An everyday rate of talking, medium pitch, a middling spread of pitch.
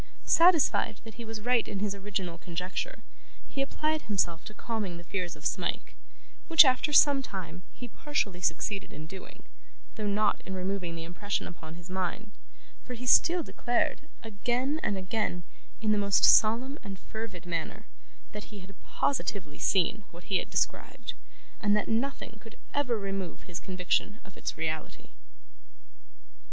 No: average, 160 wpm; high, 205 Hz; average, 4.6 semitones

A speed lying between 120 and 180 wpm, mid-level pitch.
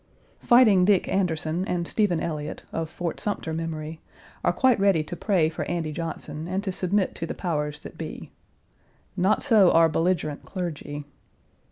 Yes: average, 160 wpm; medium, 170 Hz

